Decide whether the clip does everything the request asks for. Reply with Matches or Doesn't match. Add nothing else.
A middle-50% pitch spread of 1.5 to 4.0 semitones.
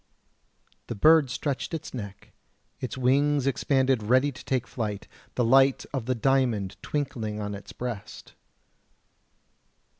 Matches